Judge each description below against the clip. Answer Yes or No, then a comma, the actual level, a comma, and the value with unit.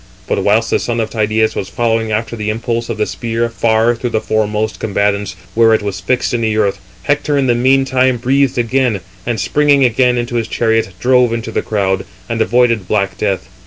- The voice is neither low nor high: No, low, 115 Hz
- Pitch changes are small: Yes, narrow, 2.2 semitones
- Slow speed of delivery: No, average, 200 wpm